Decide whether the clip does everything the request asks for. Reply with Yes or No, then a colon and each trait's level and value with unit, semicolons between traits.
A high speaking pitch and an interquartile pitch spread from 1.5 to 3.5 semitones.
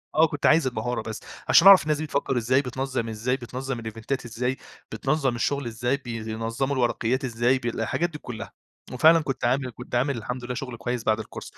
No: low, 125 Hz; average, 2.8 semitones